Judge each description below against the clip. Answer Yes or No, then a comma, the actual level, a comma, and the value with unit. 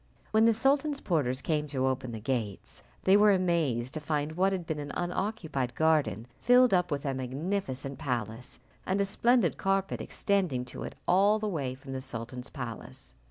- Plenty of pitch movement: Yes, wide, 7.0 semitones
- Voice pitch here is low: No, medium, 155 Hz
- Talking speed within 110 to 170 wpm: No, average, 180 wpm